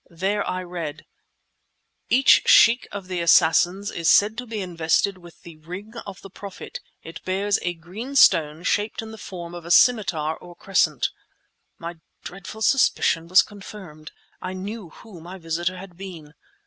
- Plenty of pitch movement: No, average, 3.3 semitones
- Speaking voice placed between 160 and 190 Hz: Yes, medium, 185 Hz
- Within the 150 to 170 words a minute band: Yes, average, 160 wpm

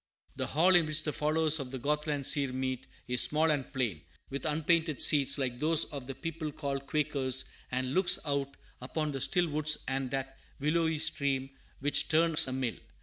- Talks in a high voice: No, medium, 145 Hz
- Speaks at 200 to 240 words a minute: No, average, 185 wpm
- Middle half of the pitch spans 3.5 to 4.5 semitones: No, average, 2.7 semitones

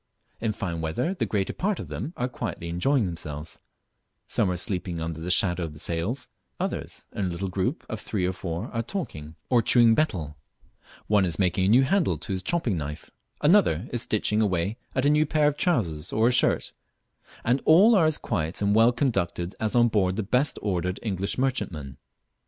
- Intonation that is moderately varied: No, wide, 6.4 semitones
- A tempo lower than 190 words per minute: No, average, 195 wpm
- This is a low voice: Yes, low, 100 Hz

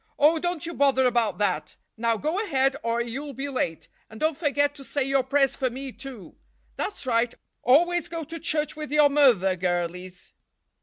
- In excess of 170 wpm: Yes, average, 185 wpm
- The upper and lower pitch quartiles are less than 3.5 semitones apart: No, average, 4.5 semitones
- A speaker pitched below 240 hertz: No, very high, 270 Hz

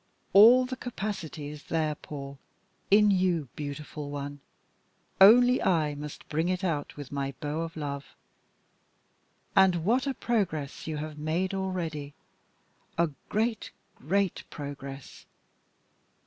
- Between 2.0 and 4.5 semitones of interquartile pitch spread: No, average, 5.0 semitones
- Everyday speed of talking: No, slow, 120 wpm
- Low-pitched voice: No, medium, 160 Hz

